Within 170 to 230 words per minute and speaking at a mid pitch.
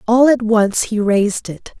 No: average, 200 wpm; high, 220 Hz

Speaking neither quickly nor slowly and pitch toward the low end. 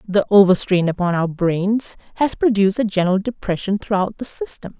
No: average, 165 wpm; high, 200 Hz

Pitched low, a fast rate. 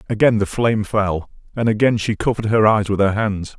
Yes: low, 105 Hz; fast, 220 wpm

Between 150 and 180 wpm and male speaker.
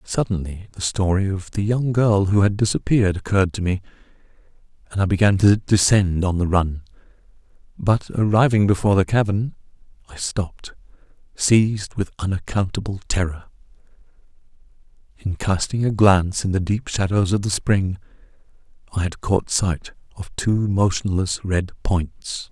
No: average, 140 wpm; male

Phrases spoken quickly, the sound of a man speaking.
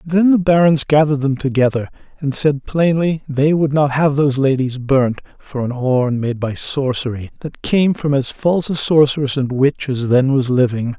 No: average, 190 wpm; male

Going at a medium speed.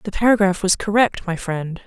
Yes: average, 195 wpm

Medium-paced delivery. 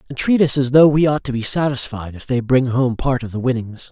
No: fast, 275 wpm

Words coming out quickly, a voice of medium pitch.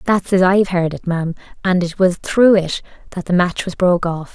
Yes: fast, 235 wpm; medium, 180 Hz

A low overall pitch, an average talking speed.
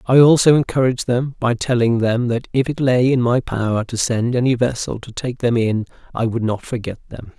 No: low, 120 Hz; fast, 220 wpm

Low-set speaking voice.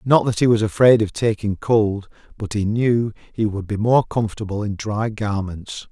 Yes: low, 110 Hz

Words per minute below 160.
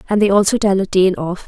No: fast, 285 wpm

